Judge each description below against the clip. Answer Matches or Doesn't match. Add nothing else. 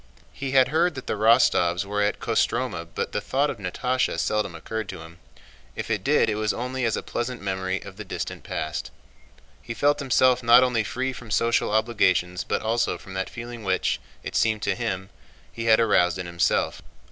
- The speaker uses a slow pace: Doesn't match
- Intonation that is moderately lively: Matches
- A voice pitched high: Doesn't match